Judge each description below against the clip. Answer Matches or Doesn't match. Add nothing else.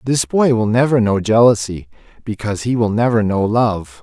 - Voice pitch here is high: Doesn't match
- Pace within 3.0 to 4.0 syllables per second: Doesn't match